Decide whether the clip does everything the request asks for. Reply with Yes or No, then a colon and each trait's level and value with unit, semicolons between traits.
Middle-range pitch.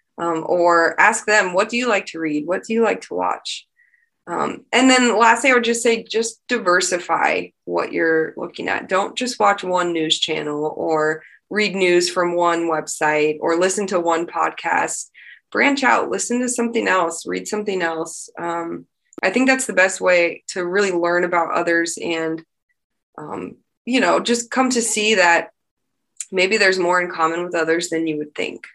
Yes: medium, 180 Hz